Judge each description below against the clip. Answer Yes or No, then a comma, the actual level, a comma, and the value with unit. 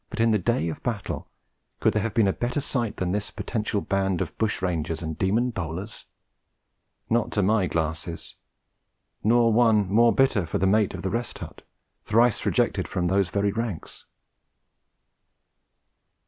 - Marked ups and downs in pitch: No, average, 3.9 semitones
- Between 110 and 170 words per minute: Yes, average, 160 wpm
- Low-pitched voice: Yes, low, 105 Hz